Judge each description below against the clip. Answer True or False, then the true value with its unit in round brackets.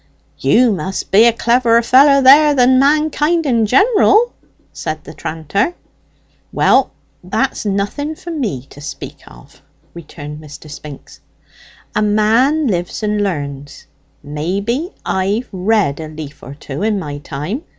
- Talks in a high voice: True (210 Hz)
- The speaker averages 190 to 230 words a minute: False (135 wpm)